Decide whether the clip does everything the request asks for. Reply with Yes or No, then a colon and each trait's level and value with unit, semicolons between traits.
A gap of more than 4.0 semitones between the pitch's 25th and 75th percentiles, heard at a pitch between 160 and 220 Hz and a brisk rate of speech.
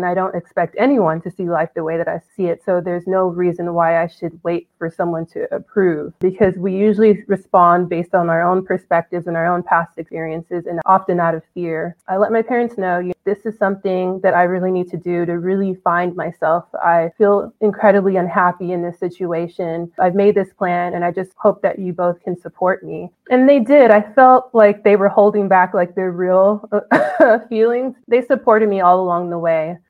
No: average, 2.7 semitones; medium, 185 Hz; fast, 210 wpm